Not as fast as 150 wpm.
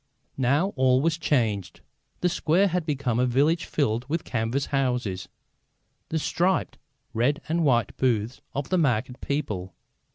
Yes: average, 140 wpm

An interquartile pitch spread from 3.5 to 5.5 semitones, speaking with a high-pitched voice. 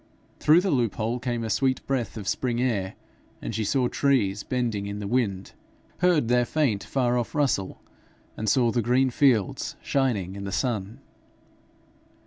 No: average, 4.1 semitones; low, 120 Hz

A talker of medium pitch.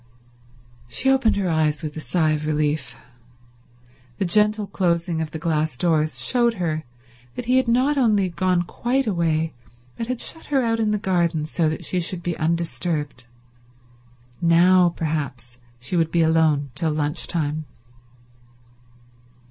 Yes: medium, 170 Hz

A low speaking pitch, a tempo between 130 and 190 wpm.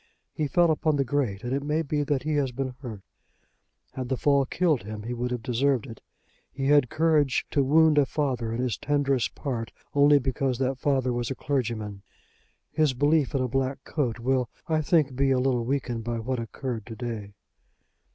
No: low, 130 Hz; average, 200 wpm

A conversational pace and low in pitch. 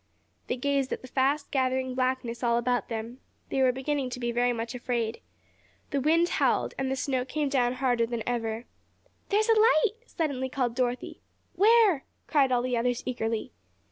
No: average, 175 wpm; very high, 255 Hz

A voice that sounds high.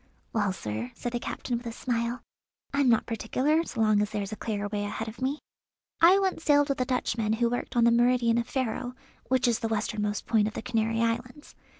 Yes: high, 235 Hz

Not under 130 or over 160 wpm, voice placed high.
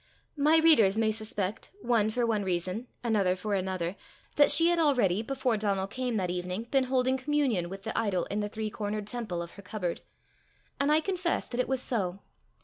No: average, 195 wpm; high, 215 Hz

